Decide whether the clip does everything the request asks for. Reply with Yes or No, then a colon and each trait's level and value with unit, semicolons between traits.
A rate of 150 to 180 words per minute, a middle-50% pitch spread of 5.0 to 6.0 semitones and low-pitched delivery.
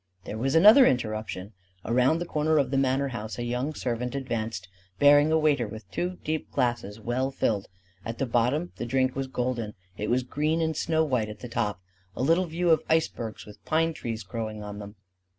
No: average, 200 wpm; wide, 5.5 semitones; low, 125 Hz